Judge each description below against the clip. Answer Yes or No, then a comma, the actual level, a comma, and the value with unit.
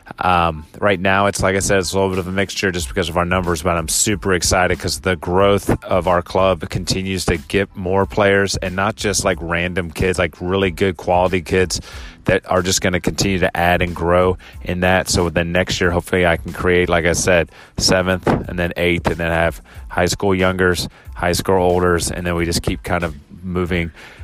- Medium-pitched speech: No, very low, 90 Hz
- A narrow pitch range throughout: Yes, narrow, 1.7 semitones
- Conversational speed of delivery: No, fast, 230 wpm